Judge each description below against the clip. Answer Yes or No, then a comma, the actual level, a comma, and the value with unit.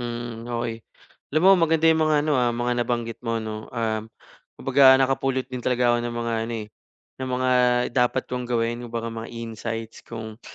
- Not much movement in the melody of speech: Yes, narrow, 1.9 semitones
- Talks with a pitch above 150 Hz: No, low, 120 Hz